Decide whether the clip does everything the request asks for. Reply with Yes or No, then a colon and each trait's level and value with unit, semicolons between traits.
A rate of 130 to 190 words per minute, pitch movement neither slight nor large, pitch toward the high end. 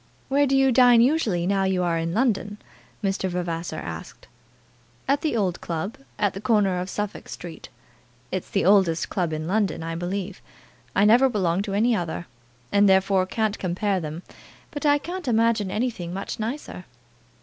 Yes: average, 170 wpm; average, 4.5 semitones; high, 195 Hz